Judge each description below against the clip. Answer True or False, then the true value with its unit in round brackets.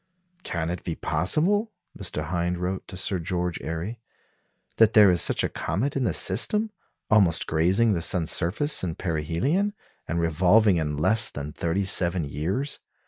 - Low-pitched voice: True (90 Hz)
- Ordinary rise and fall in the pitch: True (4.7 semitones)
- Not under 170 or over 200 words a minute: False (160 wpm)